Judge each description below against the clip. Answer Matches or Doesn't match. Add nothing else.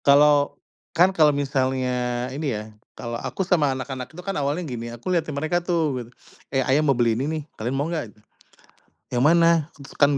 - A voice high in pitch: Doesn't match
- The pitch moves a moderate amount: Matches